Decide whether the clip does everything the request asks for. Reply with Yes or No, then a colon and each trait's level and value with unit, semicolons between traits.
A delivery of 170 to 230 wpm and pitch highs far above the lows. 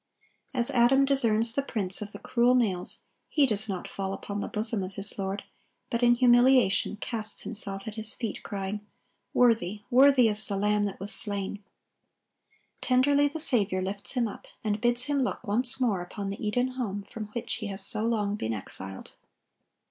No: average, 180 wpm; average, 3.5 semitones